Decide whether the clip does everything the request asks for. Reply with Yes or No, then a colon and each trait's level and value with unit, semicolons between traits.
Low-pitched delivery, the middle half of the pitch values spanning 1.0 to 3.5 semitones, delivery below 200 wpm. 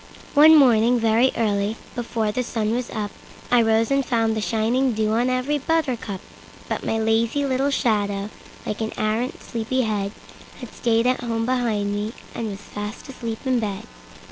No: high, 230 Hz; average, 2.8 semitones; average, 160 wpm